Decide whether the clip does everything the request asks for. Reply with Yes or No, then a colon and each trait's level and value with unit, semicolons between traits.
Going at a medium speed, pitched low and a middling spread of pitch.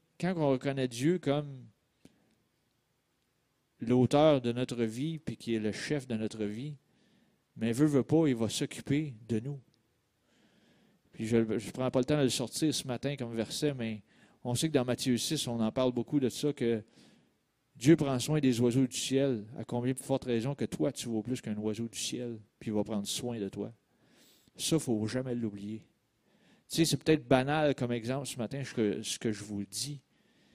Yes: average, 200 wpm; low, 125 Hz; average, 3.9 semitones